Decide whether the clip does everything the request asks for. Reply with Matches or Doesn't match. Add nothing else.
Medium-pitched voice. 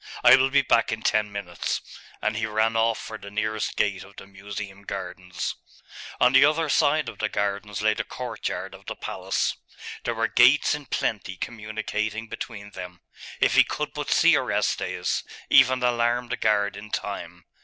Doesn't match